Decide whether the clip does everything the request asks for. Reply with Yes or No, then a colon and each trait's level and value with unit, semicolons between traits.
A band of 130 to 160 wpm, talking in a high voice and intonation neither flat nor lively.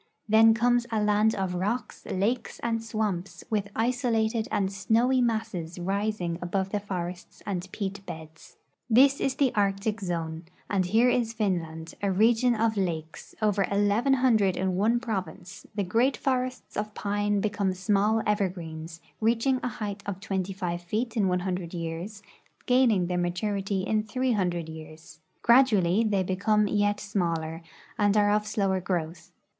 Yes: average, 145 wpm; high, 205 Hz; average, 3.6 semitones